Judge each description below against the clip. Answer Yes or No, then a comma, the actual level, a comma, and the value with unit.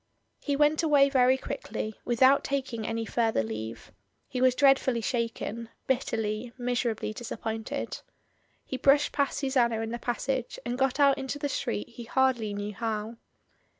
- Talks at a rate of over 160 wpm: No, average, 150 wpm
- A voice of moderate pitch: No, high, 245 Hz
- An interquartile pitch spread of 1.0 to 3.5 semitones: Yes, average, 3.2 semitones